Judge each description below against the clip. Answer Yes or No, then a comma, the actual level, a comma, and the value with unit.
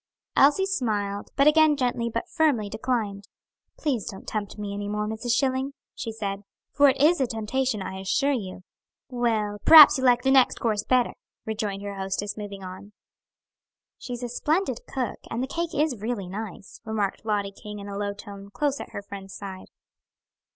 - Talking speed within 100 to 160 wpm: No, average, 180 wpm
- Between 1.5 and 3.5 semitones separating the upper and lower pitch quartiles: No, average, 4.5 semitones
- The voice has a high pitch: Yes, high, 220 Hz